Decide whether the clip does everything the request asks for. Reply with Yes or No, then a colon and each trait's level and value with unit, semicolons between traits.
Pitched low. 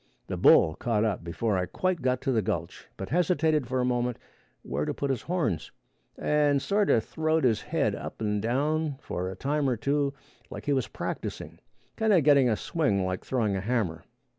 Yes: low, 125 Hz